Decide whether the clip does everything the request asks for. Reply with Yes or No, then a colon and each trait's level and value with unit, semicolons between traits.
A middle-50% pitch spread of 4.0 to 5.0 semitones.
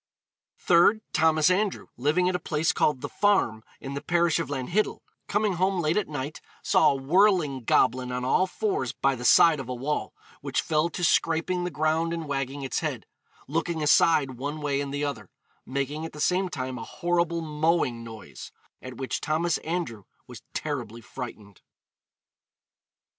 Yes: average, 4.6 semitones